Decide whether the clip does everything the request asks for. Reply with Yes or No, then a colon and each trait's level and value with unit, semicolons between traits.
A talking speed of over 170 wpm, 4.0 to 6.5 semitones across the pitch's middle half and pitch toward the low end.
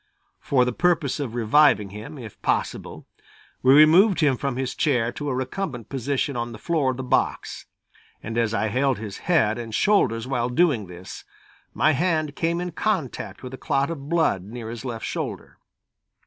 Yes: average, 180 wpm; average, 4.9 semitones; low, 130 Hz